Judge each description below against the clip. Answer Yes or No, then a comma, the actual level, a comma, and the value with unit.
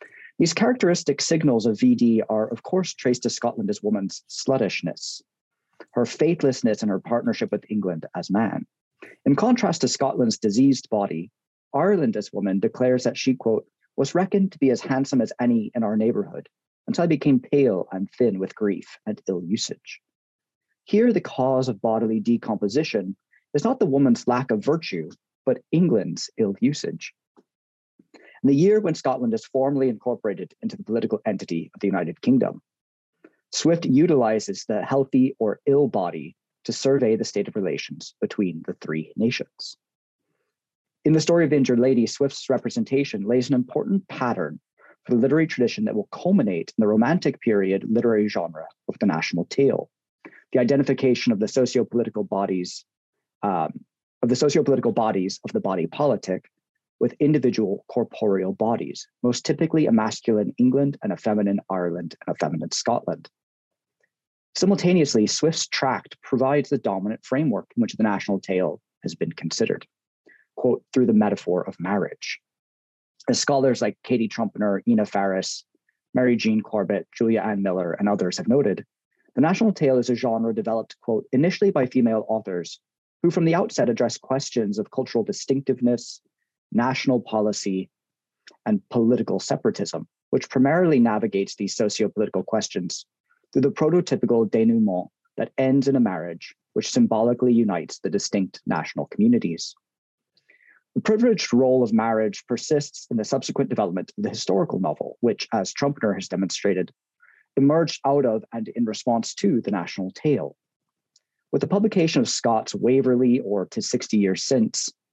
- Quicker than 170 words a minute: No, average, 155 wpm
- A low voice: Yes, low, 125 Hz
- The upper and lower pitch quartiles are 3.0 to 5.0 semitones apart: No, wide, 5.4 semitones